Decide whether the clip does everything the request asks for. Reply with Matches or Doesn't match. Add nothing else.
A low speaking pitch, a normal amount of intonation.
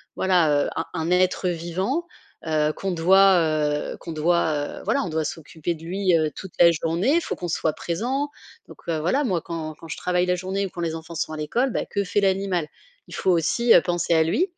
Doesn't match